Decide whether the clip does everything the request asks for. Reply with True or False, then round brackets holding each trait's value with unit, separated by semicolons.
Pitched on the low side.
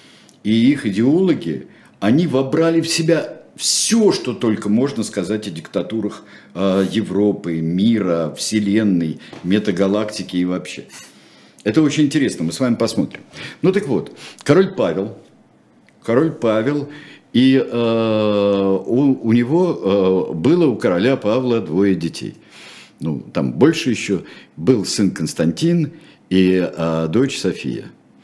True (110 Hz)